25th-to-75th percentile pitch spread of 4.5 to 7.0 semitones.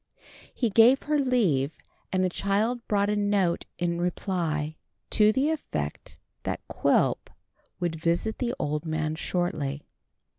Yes: wide, 5.5 semitones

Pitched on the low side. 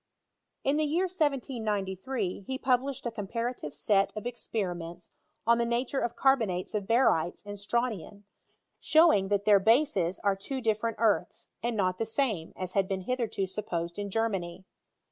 No: high, 215 Hz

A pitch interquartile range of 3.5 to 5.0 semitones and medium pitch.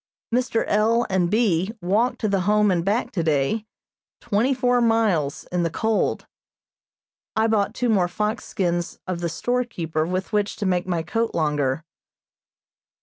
No: average, 4.6 semitones; high, 200 Hz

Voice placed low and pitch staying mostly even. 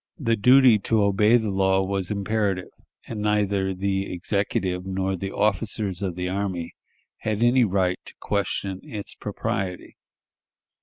Yes: low, 100 Hz; narrow, 1.8 semitones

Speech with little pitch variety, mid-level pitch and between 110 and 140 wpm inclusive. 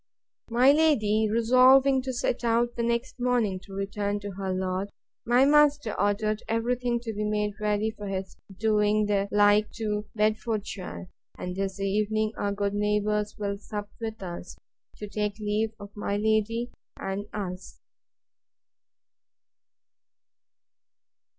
No: narrow, 2.2 semitones; high, 210 Hz; slow, 135 wpm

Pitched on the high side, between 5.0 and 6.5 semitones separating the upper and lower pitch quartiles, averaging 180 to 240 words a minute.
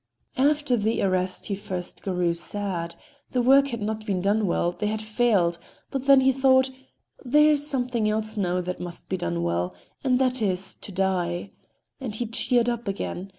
Yes: high, 210 Hz; wide, 5.5 semitones; average, 185 wpm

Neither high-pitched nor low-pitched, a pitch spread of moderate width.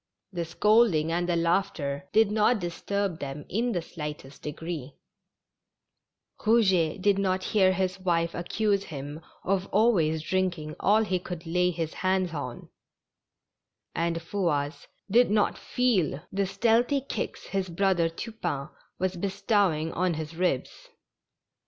Yes: medium, 180 Hz; average, 3.6 semitones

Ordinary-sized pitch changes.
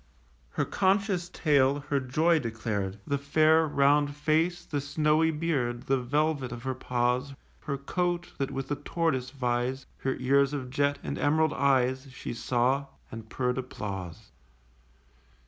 Yes: average, 3.4 semitones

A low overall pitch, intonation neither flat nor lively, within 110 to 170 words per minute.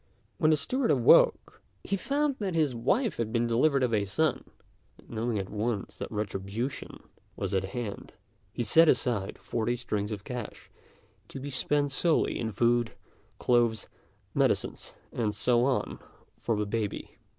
Yes: low, 120 Hz; average, 4.8 semitones; average, 155 wpm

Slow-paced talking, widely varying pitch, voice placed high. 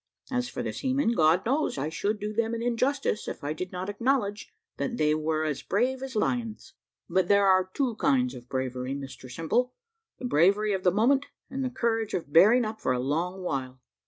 No: fast, 205 wpm; wide, 7.6 semitones; high, 205 Hz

